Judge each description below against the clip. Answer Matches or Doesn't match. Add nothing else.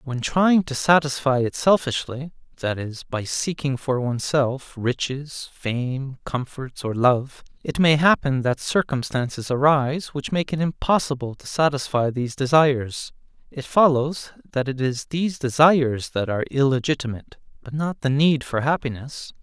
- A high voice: Doesn't match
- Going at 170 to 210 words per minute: Doesn't match